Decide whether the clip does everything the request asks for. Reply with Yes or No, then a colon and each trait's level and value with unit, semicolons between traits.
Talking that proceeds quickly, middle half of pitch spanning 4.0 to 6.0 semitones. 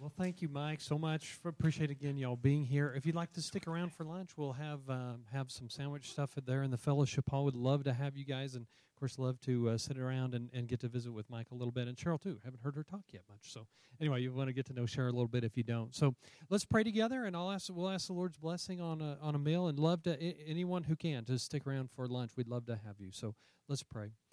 Yes: fast, 290 wpm; average, 4.5 semitones